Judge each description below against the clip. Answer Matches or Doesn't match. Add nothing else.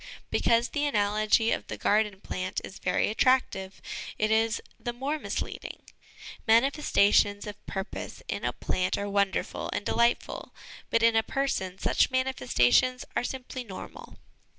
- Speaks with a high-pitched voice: Matches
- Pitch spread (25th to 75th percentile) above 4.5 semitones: Doesn't match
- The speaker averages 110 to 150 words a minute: Matches